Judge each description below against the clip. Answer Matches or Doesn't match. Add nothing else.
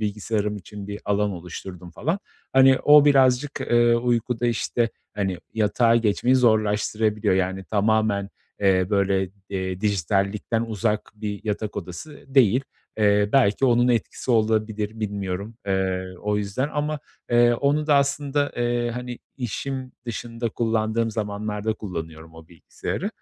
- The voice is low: Matches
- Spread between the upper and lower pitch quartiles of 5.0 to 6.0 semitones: Doesn't match